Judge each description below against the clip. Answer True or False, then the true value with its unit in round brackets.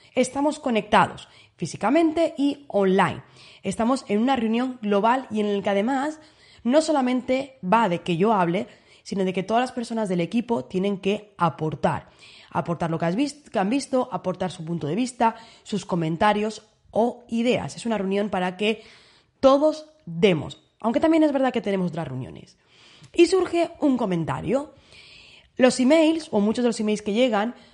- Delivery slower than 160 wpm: False (170 wpm)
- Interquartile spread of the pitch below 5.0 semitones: False (5.5 semitones)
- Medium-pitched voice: False (220 Hz)